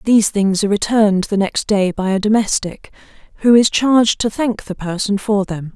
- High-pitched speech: Yes, high, 205 Hz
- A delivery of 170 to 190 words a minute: No, average, 200 wpm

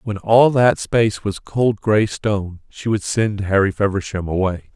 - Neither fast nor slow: Yes, average, 175 wpm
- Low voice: Yes, low, 105 Hz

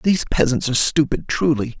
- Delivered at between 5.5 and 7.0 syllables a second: Yes, 6.0 syllables/s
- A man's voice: Yes, male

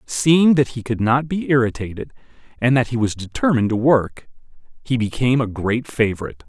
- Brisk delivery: No, average, 175 wpm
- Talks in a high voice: No, low, 120 Hz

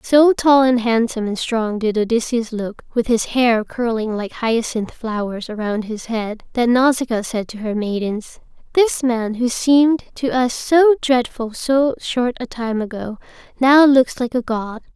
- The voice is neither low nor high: No, high, 240 Hz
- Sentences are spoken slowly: No, average, 175 wpm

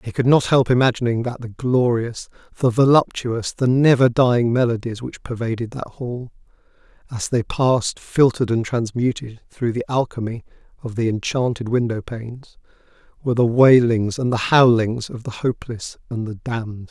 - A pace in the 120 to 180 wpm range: Yes, average, 155 wpm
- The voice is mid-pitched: No, low, 120 Hz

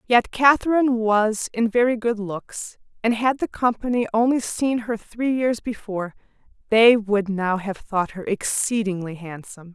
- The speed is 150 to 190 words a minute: Yes, average, 155 wpm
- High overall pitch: Yes, high, 220 Hz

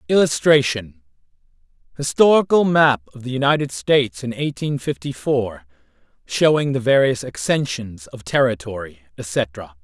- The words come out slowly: Yes, slow, 110 wpm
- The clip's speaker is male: Yes, male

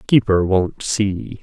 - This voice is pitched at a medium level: No, low, 100 Hz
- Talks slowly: Yes, slow, 125 wpm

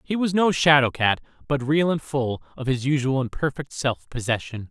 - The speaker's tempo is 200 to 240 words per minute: Yes, fast, 205 wpm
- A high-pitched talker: No, low, 135 Hz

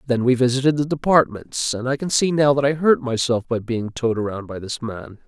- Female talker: No, male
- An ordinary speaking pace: No, fast, 240 wpm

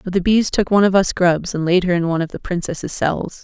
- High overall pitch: No, medium, 180 Hz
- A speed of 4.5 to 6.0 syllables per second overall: No, 6.3 syllables/s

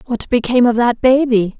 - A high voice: Yes, high, 240 Hz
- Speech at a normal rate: Yes, average, 190 wpm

